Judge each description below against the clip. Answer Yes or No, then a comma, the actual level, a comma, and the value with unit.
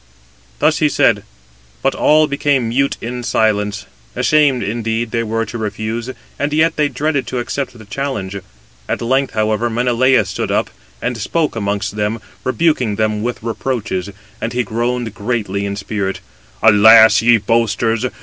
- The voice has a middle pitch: No, low, 115 Hz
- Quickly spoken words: No, average, 150 wpm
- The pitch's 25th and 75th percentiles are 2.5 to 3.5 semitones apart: Yes, average, 3.1 semitones